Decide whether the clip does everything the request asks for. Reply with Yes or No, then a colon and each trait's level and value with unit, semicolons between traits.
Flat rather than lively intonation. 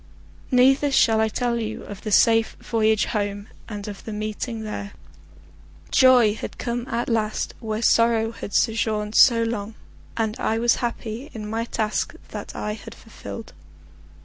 Yes: narrow, 1.7 semitones